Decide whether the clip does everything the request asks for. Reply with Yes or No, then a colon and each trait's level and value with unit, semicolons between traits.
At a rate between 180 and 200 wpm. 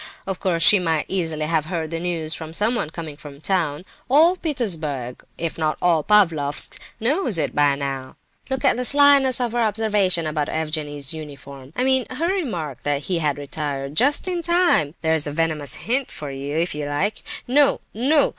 Yes: average, 185 wpm